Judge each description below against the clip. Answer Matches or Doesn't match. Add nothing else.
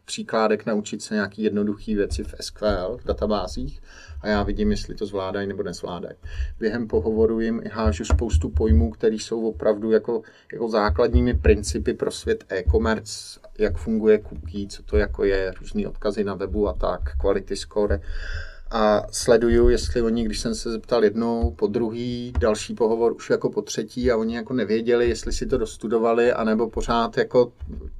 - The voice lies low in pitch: Matches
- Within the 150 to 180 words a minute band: Matches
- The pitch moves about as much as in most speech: Matches